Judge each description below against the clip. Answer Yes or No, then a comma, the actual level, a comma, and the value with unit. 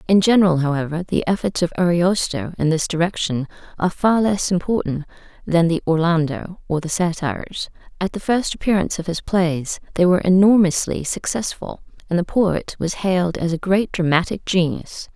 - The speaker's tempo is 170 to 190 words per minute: No, average, 160 wpm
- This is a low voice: No, medium, 175 Hz